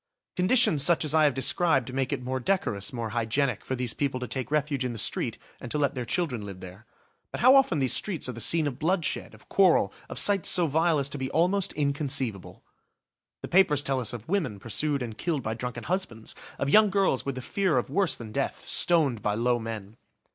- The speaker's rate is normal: No, fast, 220 wpm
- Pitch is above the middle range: No, low, 135 Hz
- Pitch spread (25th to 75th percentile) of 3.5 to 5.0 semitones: No, wide, 5.6 semitones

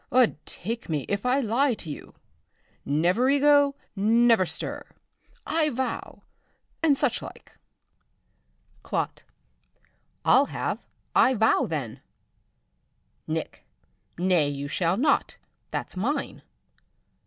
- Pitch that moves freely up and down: Yes, wide, 7.8 semitones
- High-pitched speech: Yes, high, 225 Hz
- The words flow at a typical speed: No, slow, 100 wpm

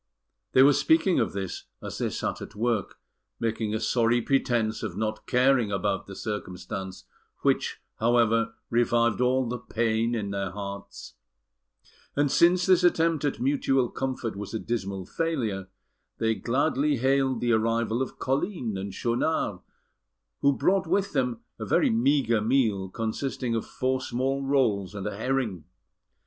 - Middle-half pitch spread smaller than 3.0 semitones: No, average, 4.0 semitones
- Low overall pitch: Yes, low, 115 Hz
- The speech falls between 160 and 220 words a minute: No, average, 150 wpm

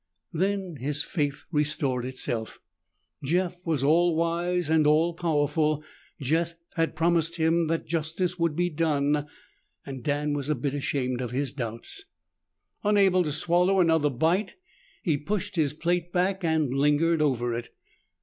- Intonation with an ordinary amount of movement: Yes, average, 3.2 semitones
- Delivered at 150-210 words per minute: No, average, 140 wpm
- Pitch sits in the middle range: Yes, medium, 160 Hz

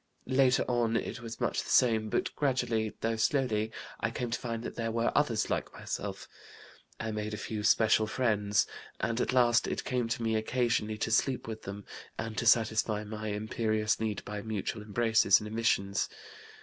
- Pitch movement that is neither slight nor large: No, narrow, 1.7 semitones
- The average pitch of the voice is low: Yes, low, 110 Hz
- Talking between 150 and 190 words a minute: Yes, average, 180 wpm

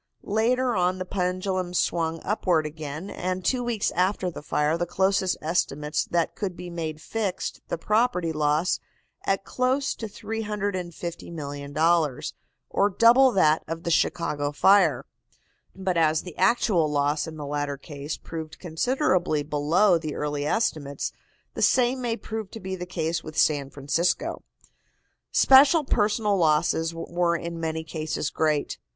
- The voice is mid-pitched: Yes, medium, 170 Hz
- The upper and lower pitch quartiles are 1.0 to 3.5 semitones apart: No, average, 4.3 semitones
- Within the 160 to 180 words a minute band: No, average, 145 wpm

